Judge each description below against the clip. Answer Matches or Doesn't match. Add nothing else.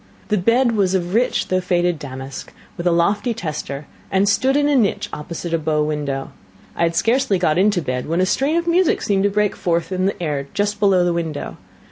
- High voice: Doesn't match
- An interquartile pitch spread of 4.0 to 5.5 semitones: Matches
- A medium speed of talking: Doesn't match